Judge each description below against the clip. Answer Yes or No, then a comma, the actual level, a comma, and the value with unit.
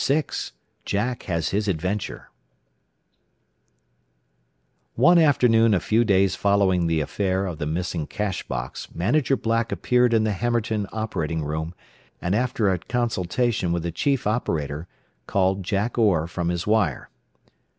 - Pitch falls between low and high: No, low, 100 Hz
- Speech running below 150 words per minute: Yes, slow, 135 wpm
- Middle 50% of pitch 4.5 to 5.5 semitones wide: Yes, average, 4.9 semitones